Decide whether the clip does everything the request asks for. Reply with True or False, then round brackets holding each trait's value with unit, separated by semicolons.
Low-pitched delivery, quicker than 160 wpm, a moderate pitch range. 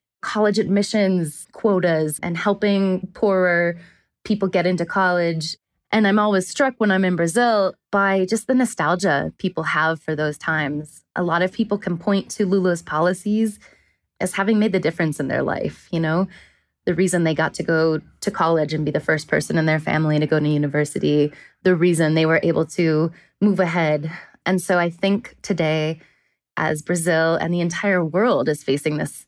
False (175 Hz; 180 wpm; 3.7 semitones)